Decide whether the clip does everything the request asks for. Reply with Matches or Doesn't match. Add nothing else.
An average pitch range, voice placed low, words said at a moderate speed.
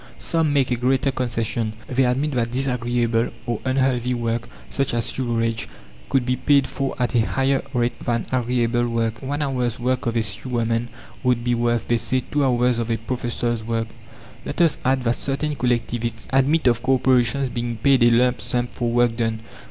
Doesn't match